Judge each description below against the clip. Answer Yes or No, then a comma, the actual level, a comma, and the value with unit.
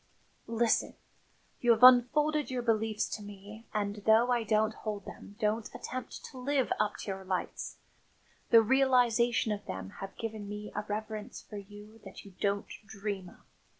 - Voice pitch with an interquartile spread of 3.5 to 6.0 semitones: No, narrow, 2.6 semitones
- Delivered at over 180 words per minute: No, average, 165 wpm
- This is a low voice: No, high, 215 Hz